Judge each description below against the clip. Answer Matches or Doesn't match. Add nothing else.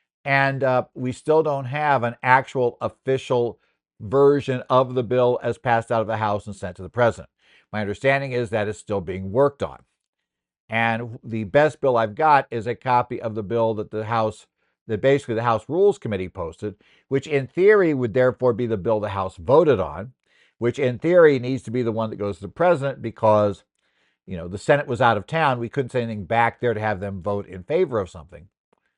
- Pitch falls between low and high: Doesn't match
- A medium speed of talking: Doesn't match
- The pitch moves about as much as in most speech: Matches